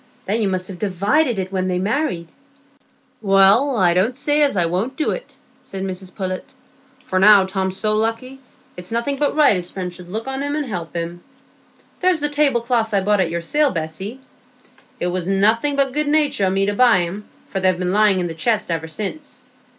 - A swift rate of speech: Yes, fast, 210 wpm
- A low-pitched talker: No, high, 200 Hz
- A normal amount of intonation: No, wide, 5.9 semitones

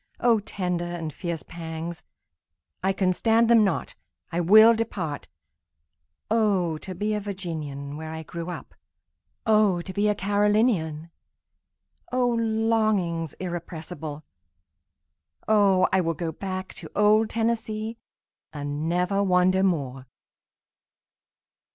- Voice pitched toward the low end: No, medium, 185 Hz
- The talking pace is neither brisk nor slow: No, slow, 105 wpm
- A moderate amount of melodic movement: Yes, average, 4.7 semitones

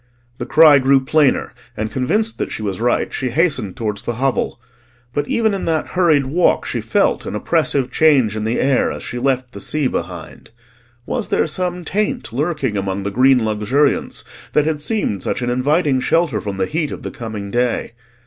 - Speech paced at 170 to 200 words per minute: Yes, average, 190 wpm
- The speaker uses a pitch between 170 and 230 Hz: No, low, 135 Hz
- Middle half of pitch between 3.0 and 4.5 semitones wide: No, wide, 5.6 semitones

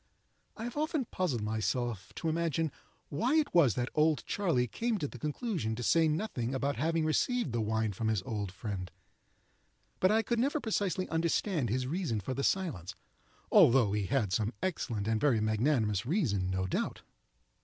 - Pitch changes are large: Yes, wide, 8.5 semitones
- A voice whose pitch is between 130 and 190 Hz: Yes, low, 135 Hz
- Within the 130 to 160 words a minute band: No, average, 175 wpm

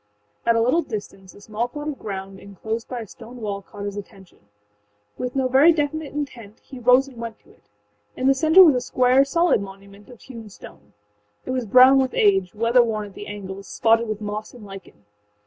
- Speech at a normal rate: No, fast, 215 wpm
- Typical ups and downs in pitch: Yes, average, 4.2 semitones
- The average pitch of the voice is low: No, high, 230 Hz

